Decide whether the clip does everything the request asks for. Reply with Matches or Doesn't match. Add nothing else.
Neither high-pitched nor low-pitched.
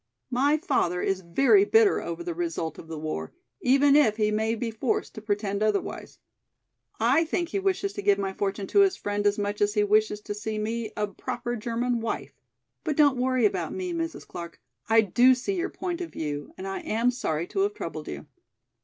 Doesn't match